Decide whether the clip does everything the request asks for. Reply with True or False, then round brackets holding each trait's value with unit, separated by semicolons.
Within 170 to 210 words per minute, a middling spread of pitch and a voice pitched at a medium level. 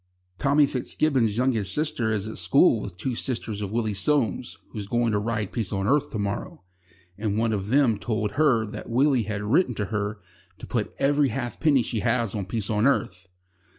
False (190 wpm; 3.9 semitones; 110 Hz)